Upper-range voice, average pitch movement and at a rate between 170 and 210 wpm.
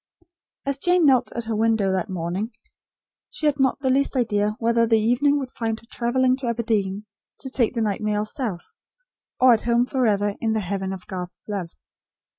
Yes: high, 225 Hz; average, 3.8 semitones; average, 190 wpm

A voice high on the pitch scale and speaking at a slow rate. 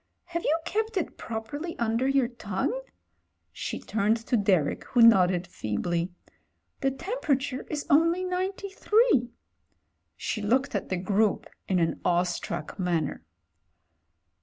Yes: high, 235 Hz; slow, 120 wpm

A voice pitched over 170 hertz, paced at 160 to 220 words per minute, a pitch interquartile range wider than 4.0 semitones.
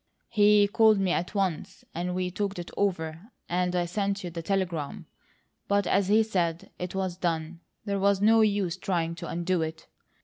No: medium, 185 Hz; average, 180 wpm; average, 2.8 semitones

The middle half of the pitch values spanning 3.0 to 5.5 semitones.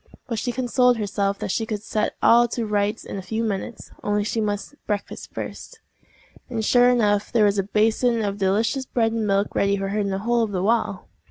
No: narrow, 2.5 semitones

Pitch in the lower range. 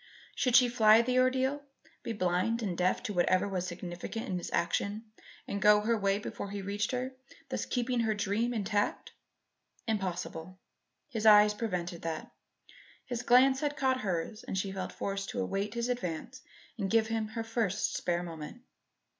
No: high, 210 Hz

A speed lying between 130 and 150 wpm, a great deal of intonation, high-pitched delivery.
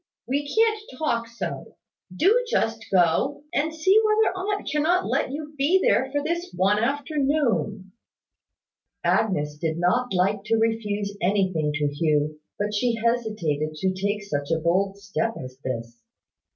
Yes: average, 145 wpm; wide, 8.8 semitones; high, 210 Hz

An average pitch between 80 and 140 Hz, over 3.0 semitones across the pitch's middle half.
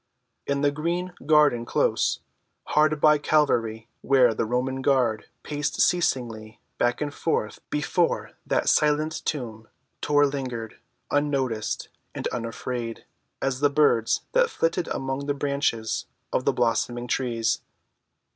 Yes: low, 135 Hz; average, 4.1 semitones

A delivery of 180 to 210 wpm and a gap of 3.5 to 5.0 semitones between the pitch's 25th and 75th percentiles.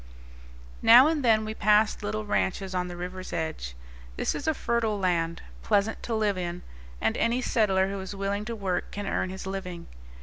No: average, 190 wpm; average, 3.1 semitones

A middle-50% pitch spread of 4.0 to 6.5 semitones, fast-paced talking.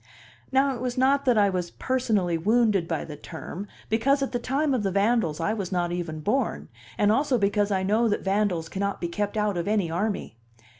Yes: average, 5.3 semitones; fast, 210 wpm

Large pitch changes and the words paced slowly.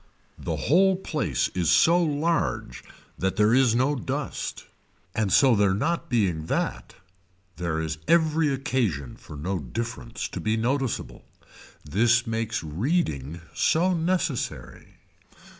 Yes: wide, 8.4 semitones; slow, 125 wpm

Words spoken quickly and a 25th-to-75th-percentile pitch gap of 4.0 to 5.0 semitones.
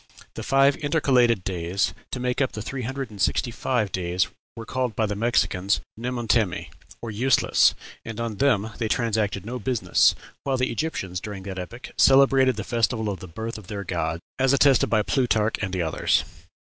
No: average, 180 wpm; average, 4.4 semitones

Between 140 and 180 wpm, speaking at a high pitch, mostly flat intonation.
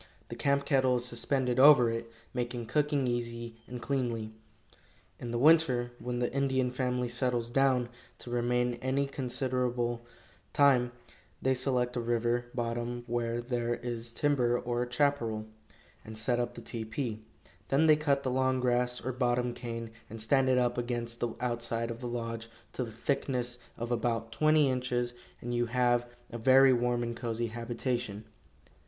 No: average, 160 wpm; low, 120 Hz; narrow, 1.6 semitones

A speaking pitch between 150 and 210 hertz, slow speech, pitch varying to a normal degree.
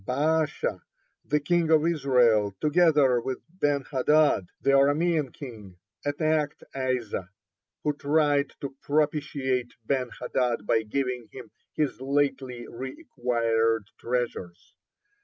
No: low, 135 Hz; slow, 110 wpm; average, 3.7 semitones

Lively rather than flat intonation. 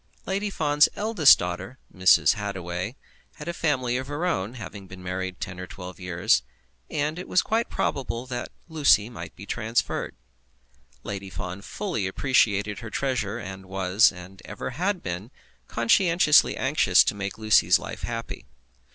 Yes: wide, 7.4 semitones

